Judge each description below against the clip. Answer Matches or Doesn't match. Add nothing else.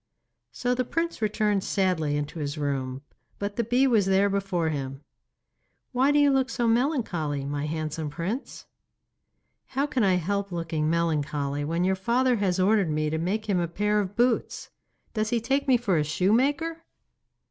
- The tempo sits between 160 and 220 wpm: Matches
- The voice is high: Matches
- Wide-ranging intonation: Matches